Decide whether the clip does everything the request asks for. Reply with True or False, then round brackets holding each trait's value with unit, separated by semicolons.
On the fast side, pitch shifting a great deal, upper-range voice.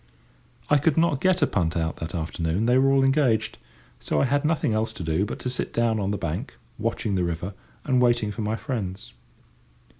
False (210 wpm; 6.7 semitones; 110 Hz)